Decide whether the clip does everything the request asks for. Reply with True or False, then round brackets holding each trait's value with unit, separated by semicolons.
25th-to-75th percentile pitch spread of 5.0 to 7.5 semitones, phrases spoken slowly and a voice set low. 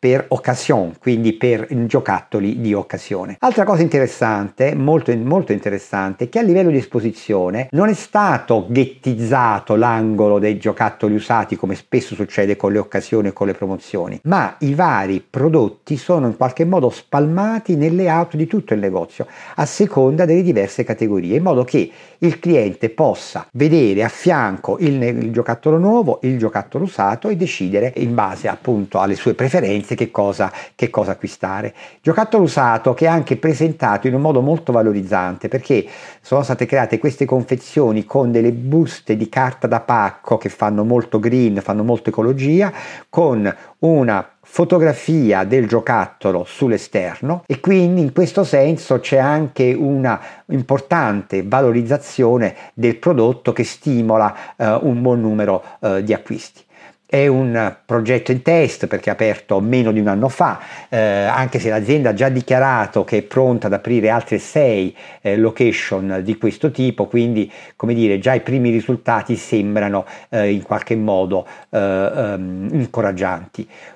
False (5.5 semitones; 155 wpm; 125 Hz)